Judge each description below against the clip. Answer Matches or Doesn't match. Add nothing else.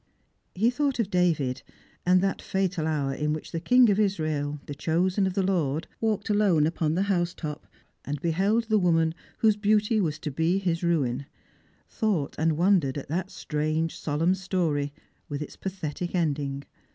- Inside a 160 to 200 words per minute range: Matches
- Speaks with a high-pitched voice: Doesn't match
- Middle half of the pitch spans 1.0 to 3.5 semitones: Doesn't match